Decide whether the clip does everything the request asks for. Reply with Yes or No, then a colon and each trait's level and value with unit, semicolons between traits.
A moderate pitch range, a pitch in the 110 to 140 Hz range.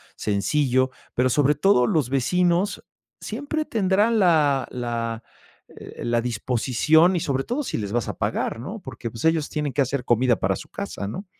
No: wide, 6.7 semitones; low, 135 Hz